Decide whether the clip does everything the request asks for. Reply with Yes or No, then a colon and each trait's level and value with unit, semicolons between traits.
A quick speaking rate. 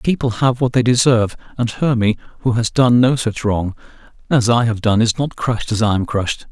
Yes: fast, 230 wpm